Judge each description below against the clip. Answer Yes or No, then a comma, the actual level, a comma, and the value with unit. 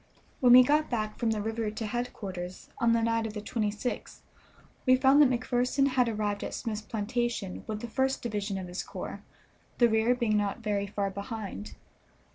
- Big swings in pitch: No, average, 2.8 semitones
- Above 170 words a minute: Yes, average, 185 wpm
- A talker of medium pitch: No, high, 225 Hz